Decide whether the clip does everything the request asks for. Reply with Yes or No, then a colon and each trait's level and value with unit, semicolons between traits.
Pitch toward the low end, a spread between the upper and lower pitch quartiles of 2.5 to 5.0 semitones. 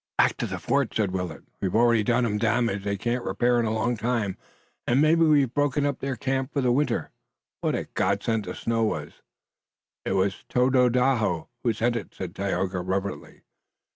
Yes: low, 115 Hz; average, 4.0 semitones